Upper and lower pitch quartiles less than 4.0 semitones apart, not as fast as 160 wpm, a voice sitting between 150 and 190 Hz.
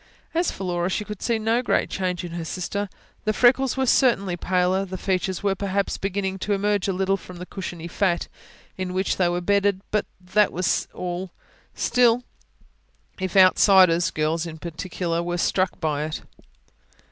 No: narrow, 2.4 semitones; average, 175 wpm; medium, 185 Hz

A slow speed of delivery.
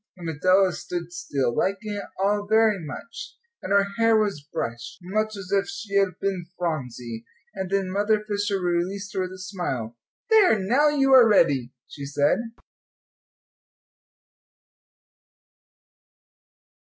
Yes: slow, 130 wpm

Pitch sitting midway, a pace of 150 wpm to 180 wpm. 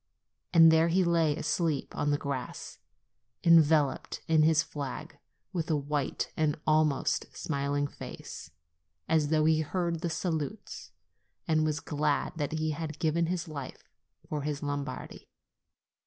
No: medium, 155 Hz; average, 140 wpm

